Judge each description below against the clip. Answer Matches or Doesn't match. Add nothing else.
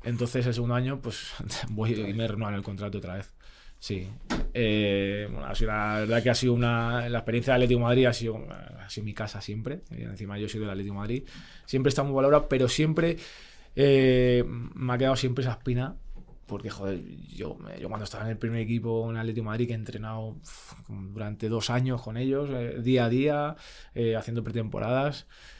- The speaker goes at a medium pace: Doesn't match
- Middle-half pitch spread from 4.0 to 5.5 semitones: Doesn't match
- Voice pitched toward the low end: Matches